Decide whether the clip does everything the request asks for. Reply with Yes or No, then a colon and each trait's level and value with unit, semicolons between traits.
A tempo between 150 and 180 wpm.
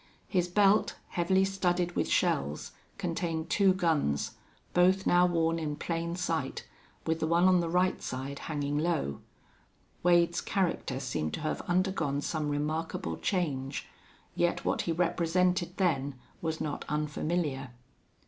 No: slow, 135 wpm